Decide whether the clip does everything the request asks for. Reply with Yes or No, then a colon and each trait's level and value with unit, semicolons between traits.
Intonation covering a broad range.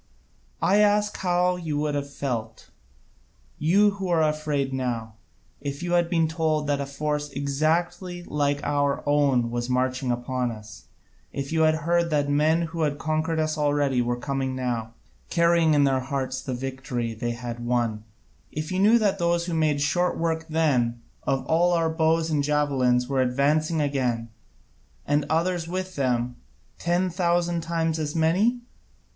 No: average, 4.1 semitones